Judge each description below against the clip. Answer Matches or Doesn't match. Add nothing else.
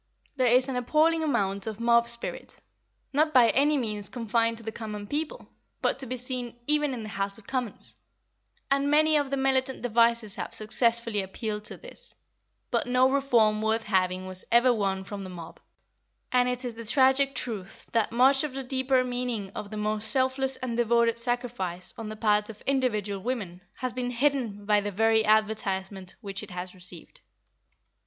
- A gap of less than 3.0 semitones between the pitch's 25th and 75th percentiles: Doesn't match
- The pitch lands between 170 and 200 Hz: Doesn't match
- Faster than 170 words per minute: Matches